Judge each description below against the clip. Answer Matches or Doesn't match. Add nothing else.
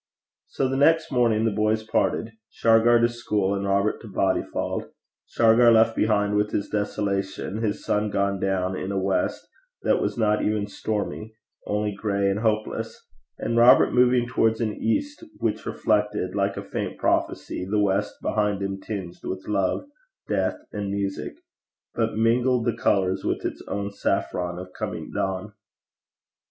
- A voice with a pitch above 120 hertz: Doesn't match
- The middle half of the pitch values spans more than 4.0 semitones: Doesn't match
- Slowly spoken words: Doesn't match